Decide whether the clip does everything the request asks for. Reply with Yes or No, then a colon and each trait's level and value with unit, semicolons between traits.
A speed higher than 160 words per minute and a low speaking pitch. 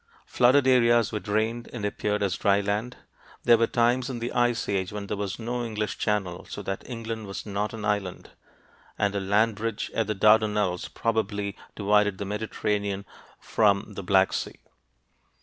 Yes: average, 170 wpm; low, 105 Hz